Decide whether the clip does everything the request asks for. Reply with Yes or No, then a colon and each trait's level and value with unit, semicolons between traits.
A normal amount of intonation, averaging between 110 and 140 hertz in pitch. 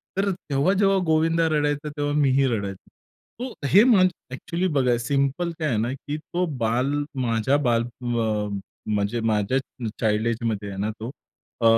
No: wide, 5.8 semitones; low, 135 Hz